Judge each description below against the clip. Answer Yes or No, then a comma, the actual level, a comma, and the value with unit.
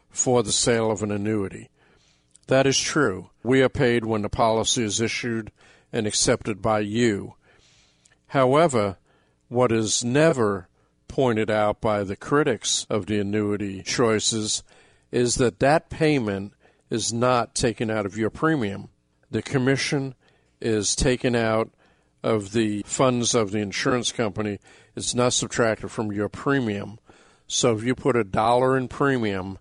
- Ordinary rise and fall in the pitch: Yes, average, 3.3 semitones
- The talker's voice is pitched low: Yes, low, 110 Hz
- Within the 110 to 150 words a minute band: Yes, average, 145 wpm